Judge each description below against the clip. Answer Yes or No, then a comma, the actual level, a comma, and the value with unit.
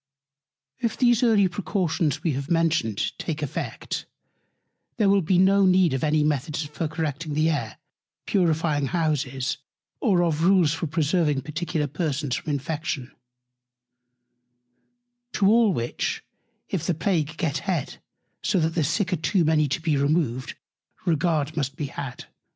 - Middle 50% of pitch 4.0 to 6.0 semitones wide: No, average, 3.4 semitones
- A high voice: No, medium, 160 Hz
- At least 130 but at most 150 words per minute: Yes, average, 145 wpm